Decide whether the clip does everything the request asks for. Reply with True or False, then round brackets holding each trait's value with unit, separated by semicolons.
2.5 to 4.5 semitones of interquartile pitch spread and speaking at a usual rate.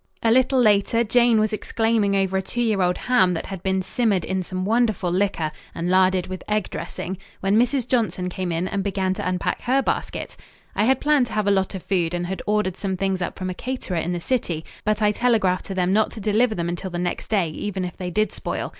False (3.2 semitones; 240 wpm)